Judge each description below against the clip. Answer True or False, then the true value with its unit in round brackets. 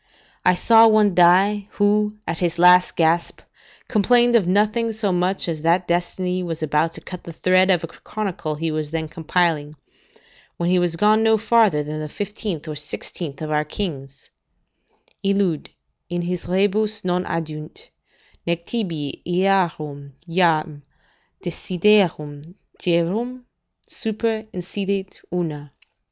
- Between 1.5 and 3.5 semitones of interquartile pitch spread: False (4.3 semitones)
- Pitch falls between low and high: True (180 Hz)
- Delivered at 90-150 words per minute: True (135 wpm)